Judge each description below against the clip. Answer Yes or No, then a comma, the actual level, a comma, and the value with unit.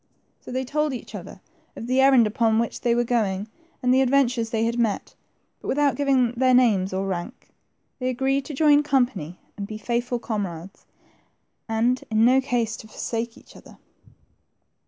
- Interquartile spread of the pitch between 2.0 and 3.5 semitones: Yes, average, 3.1 semitones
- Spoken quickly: No, average, 175 wpm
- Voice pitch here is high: Yes, high, 240 Hz